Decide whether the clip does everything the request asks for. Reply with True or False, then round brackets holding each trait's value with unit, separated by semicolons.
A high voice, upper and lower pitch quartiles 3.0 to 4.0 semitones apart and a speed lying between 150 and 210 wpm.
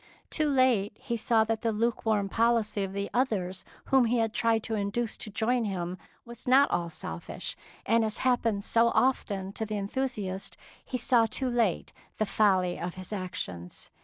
True (220 Hz; 3.3 semitones; 175 wpm)